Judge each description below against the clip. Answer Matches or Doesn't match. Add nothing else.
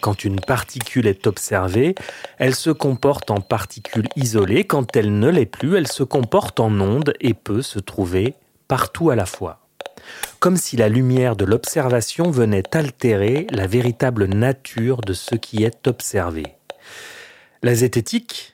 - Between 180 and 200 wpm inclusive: Doesn't match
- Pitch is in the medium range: Doesn't match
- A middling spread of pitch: Matches